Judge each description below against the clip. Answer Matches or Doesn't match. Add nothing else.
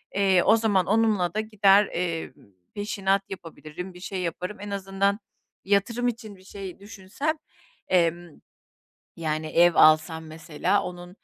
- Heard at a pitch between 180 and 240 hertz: Matches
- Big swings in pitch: Doesn't match